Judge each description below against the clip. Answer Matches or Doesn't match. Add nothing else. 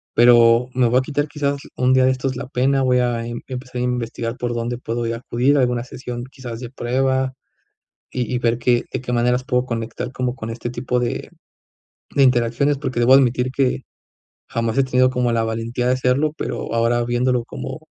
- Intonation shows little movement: Matches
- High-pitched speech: Doesn't match